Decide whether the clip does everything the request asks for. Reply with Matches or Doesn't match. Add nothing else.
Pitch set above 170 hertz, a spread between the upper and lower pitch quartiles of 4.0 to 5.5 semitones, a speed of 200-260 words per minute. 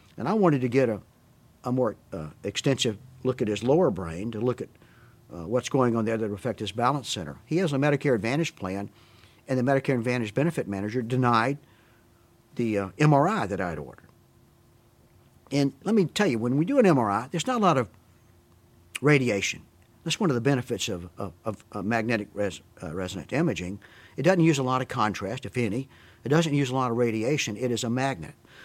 Doesn't match